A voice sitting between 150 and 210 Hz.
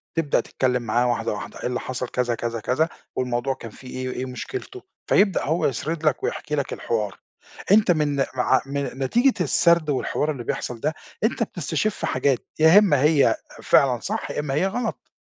No: medium, 140 Hz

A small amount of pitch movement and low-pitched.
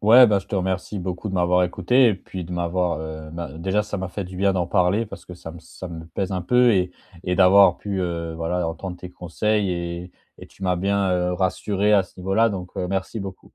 Yes: narrow, 2.1 semitones; very low, 90 Hz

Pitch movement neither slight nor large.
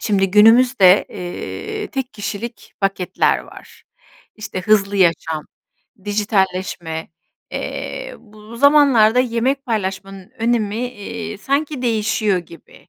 Yes: average, 4.0 semitones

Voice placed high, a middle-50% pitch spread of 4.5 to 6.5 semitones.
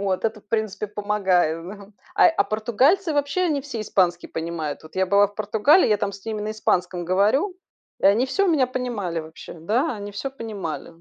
Yes: high, 210 Hz; average, 5.2 semitones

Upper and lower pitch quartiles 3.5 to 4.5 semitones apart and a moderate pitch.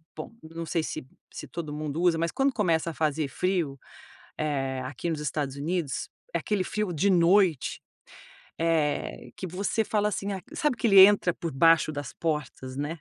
Yes: average, 4.0 semitones; medium, 165 Hz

